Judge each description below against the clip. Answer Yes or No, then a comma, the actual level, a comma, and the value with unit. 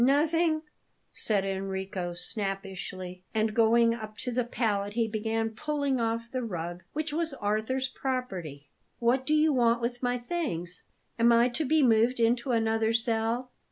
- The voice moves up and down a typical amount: Yes, average, 3.7 semitones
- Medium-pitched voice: No, high, 230 Hz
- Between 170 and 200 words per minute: No, average, 155 wpm